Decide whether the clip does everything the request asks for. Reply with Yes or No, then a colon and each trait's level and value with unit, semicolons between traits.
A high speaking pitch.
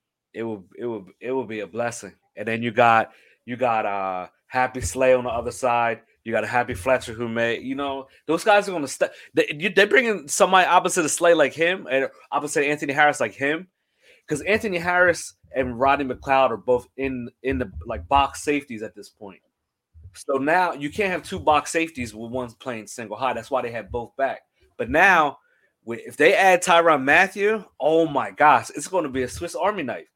No: low, 130 Hz